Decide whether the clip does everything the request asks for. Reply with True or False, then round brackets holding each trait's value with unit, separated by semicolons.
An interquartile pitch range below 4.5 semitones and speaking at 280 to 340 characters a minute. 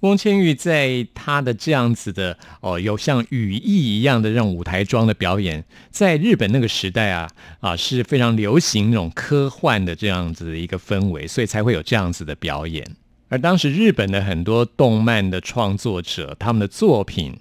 False (5.2 semitones; 285 characters per minute)